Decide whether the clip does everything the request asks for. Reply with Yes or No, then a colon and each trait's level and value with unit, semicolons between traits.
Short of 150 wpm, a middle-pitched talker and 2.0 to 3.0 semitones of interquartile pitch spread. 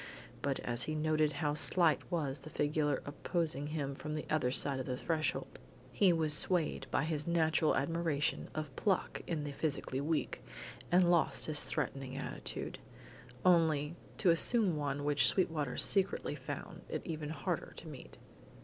No: average, 160 wpm; medium, 155 Hz; narrow, 2.6 semitones